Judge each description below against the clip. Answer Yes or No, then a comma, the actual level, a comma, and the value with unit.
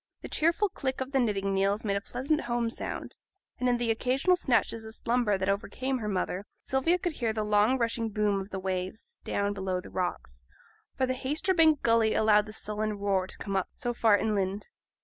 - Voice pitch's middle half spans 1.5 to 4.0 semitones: No, average, 4.4 semitones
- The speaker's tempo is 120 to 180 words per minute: No, fast, 205 wpm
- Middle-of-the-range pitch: No, high, 220 Hz